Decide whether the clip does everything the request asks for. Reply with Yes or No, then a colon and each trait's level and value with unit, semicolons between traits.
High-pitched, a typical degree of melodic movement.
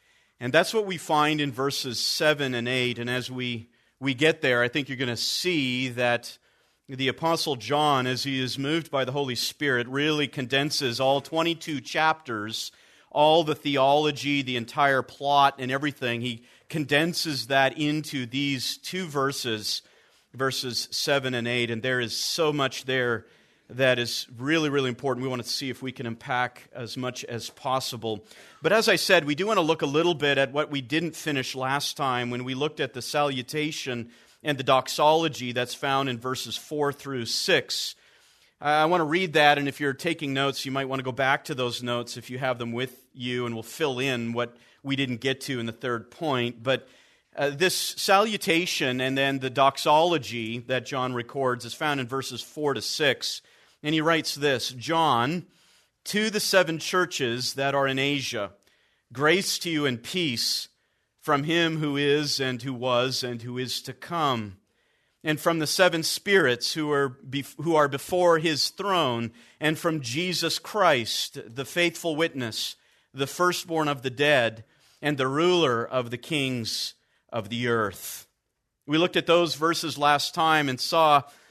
No: low, 135 Hz; average, 3.7 semitones